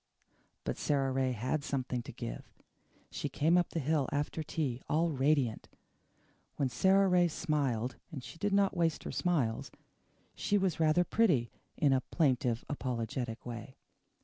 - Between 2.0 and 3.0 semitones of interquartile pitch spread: No, average, 4.8 semitones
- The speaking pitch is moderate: Yes, medium, 145 Hz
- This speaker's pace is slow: No, average, 150 wpm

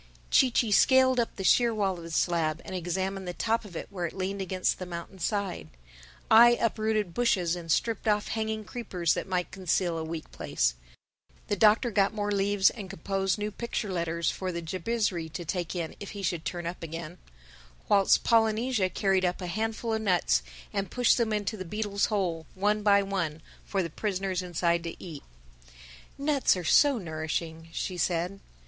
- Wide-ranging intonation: No, average, 3.7 semitones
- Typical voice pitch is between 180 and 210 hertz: Yes, high, 190 Hz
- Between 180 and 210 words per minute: Yes, average, 185 wpm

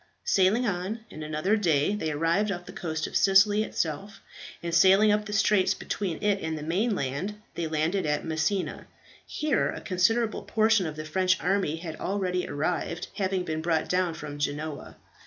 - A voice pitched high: No, medium, 180 Hz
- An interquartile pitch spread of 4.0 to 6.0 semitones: Yes, average, 4.3 semitones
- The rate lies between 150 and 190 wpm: Yes, average, 175 wpm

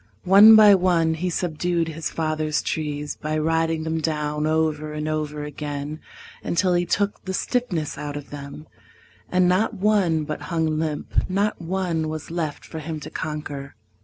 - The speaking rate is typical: Yes, average, 160 wpm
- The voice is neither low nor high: Yes, medium, 160 Hz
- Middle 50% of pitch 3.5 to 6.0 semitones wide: No, average, 2.8 semitones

